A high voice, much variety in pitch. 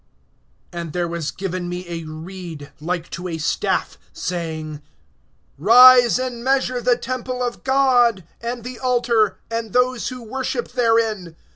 Yes: high, 225 Hz; wide, 6.3 semitones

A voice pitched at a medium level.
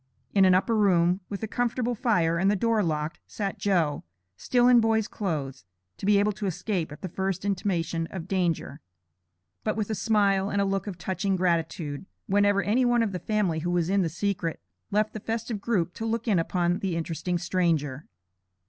No: high, 195 Hz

